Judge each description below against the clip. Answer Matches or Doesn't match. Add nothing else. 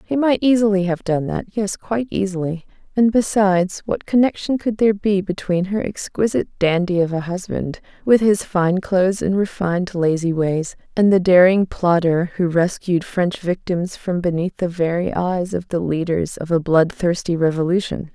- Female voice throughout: Matches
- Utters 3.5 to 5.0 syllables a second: Matches